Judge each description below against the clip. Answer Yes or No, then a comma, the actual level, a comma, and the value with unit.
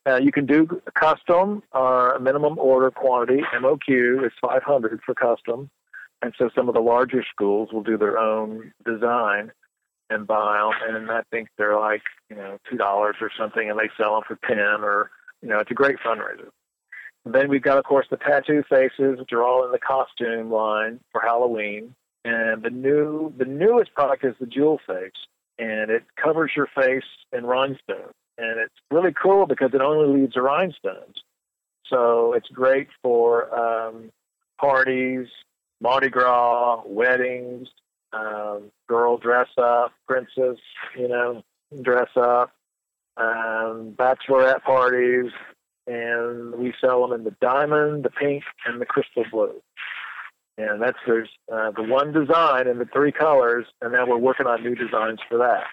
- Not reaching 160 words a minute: No, average, 165 wpm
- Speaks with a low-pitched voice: Yes, low, 125 Hz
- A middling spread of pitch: Yes, average, 3.0 semitones